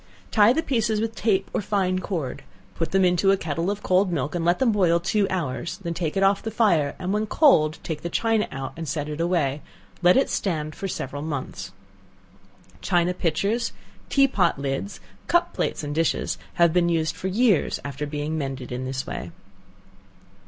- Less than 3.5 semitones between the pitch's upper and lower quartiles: No, average, 5.0 semitones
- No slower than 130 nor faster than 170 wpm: No, average, 190 wpm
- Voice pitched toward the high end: No, medium, 175 Hz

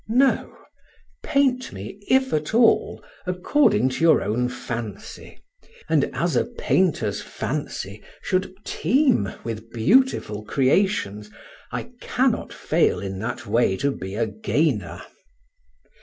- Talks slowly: Yes, slow, 115 wpm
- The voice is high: No, low, 130 Hz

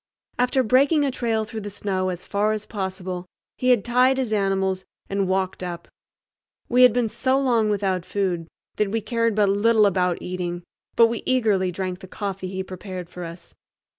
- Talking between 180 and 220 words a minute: Yes, average, 185 wpm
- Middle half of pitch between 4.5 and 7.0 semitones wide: No, average, 3.7 semitones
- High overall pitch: Yes, high, 200 Hz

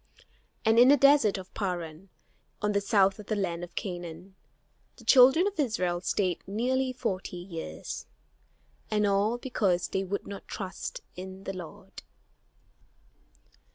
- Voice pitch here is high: Yes, high, 195 Hz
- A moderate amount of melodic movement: Yes, average, 3.8 semitones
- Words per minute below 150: Yes, average, 140 wpm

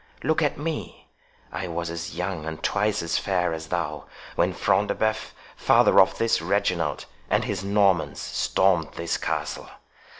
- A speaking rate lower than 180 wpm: Yes, average, 155 wpm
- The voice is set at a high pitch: No, very low, 90 Hz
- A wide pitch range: No, average, 3.6 semitones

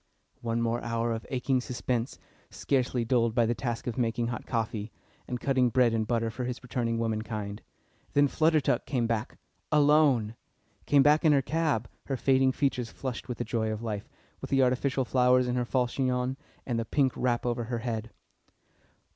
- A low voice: Yes, low, 125 Hz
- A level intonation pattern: Yes, narrow, 2.3 semitones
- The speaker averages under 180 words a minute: No, average, 185 wpm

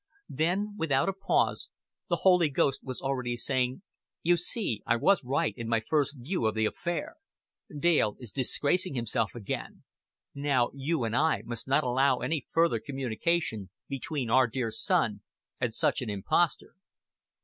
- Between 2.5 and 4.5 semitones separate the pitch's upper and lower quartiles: No, average, 5.2 semitones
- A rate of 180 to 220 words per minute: No, average, 155 wpm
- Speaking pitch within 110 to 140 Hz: Yes, low, 135 Hz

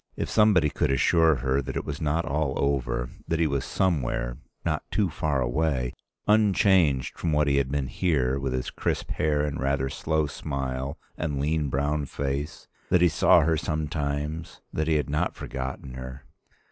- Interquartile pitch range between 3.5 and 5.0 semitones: No, average, 2.8 semitones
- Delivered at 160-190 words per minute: Yes, average, 175 wpm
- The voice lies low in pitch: Yes, very low, 75 Hz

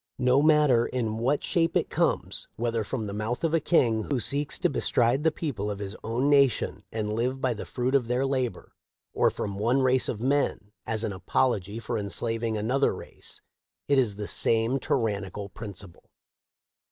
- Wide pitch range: No, average, 4.0 semitones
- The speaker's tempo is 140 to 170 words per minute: No, average, 180 wpm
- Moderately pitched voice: No, low, 120 Hz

